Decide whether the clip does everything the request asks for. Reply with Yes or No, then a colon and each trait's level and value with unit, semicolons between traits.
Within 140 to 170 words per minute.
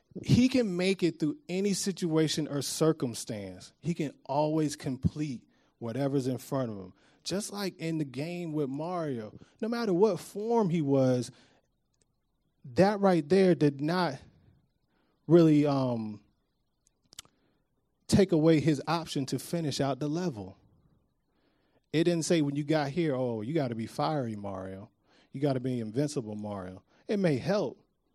Yes: average, 150 wpm